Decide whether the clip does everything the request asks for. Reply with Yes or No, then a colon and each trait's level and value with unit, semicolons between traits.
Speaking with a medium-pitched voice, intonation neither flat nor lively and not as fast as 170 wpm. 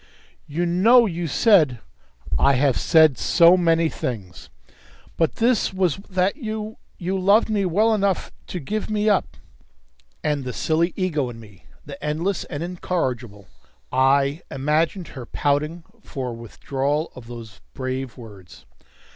No: medium, 160 Hz; wide, 6.1 semitones; average, 145 wpm